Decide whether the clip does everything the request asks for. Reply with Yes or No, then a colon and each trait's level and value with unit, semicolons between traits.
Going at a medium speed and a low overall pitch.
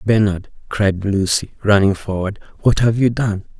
Yes: average, 150 wpm; low, 105 Hz